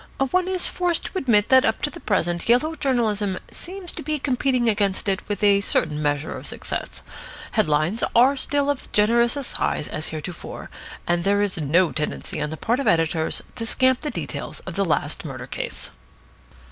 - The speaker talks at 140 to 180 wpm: No, average, 190 wpm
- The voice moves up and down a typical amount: No, wide, 7.8 semitones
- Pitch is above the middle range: Yes, high, 215 Hz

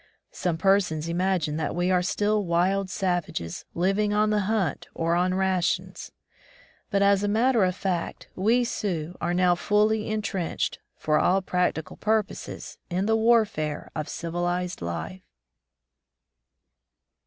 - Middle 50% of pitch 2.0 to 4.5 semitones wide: Yes, average, 3.3 semitones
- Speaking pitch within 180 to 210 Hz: Yes, medium, 185 Hz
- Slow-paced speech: Yes, slow, 130 wpm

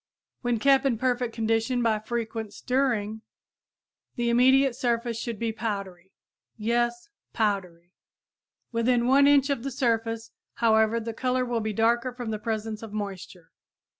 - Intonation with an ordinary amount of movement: No, narrow, 2.1 semitones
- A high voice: Yes, high, 230 Hz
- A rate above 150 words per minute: No, average, 140 wpm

